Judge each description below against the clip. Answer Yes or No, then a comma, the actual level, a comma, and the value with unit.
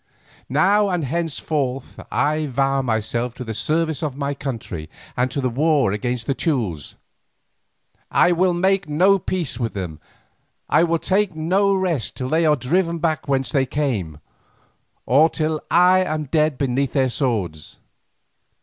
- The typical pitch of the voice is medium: Yes, medium, 145 Hz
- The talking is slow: No, average, 150 wpm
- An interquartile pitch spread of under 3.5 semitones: No, average, 4.9 semitones